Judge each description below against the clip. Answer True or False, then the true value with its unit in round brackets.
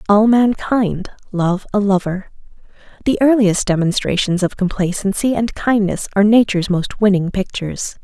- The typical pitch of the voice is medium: False (200 Hz)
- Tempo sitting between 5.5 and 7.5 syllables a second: False (5.0 syllables/s)